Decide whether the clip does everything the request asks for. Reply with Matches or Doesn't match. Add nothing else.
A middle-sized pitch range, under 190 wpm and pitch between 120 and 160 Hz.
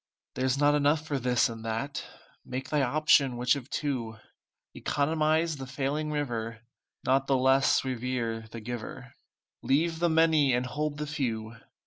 Matches